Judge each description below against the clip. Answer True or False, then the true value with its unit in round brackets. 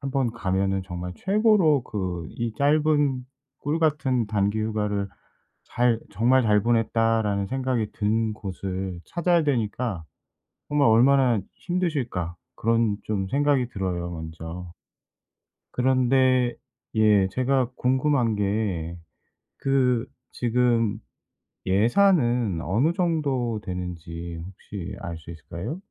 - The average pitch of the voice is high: False (115 Hz)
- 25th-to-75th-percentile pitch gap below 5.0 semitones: False (5.3 semitones)